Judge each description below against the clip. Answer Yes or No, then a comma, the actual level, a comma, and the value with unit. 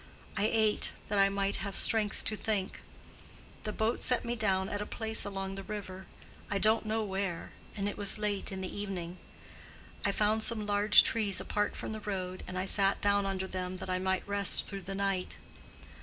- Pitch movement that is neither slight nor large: No, narrow, 1.8 semitones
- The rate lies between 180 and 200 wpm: Yes, average, 190 wpm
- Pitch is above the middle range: Yes, high, 200 Hz